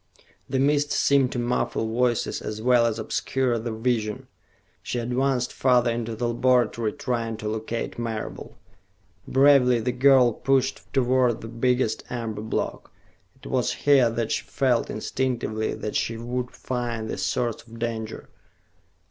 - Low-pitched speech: Yes, low, 120 Hz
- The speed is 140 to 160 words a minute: Yes, average, 145 wpm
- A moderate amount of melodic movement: No, narrow, 2.0 semitones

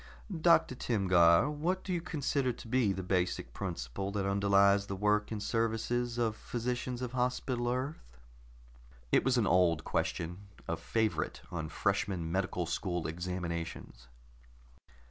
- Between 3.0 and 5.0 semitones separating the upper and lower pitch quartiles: No, wide, 5.5 semitones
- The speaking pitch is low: Yes, low, 100 Hz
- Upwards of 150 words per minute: No, slow, 135 wpm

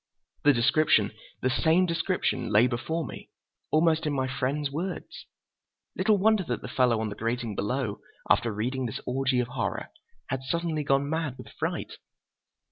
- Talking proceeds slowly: No, average, 150 wpm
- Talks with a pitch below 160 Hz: Yes, low, 135 Hz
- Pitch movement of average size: Yes, average, 5.0 semitones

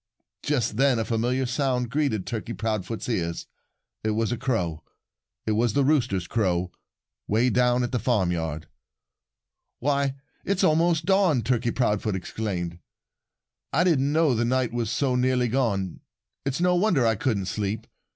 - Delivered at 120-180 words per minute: Yes, average, 150 wpm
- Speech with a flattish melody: No, average, 4.2 semitones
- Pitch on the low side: Yes, low, 120 Hz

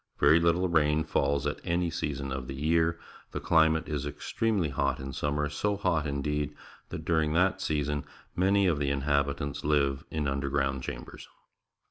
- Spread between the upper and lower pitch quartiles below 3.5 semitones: Yes, average, 2.8 semitones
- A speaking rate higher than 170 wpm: No, average, 160 wpm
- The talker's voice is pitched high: No, very low, 75 Hz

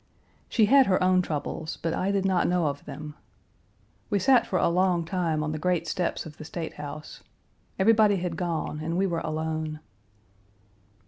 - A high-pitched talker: No, medium, 170 Hz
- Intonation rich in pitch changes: No, average, 3.1 semitones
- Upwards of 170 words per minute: Yes, average, 180 wpm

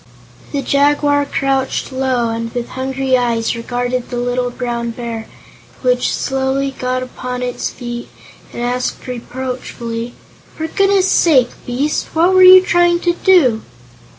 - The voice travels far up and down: No, average, 2.9 semitones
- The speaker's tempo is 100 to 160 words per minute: Yes, slow, 135 wpm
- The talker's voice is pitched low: No, very high, 255 Hz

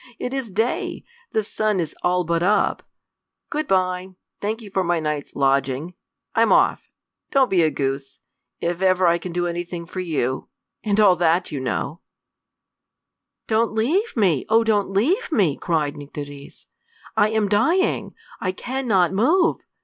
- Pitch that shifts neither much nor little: Yes, average, 4.8 semitones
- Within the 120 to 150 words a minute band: No, average, 160 wpm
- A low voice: No, medium, 185 Hz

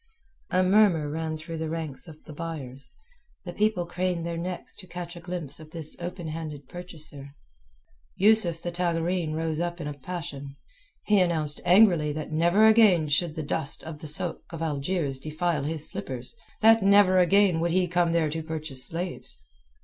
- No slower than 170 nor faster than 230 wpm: Yes, average, 175 wpm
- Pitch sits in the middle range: Yes, medium, 165 Hz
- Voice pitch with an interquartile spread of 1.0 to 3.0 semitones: Yes, narrow, 2.6 semitones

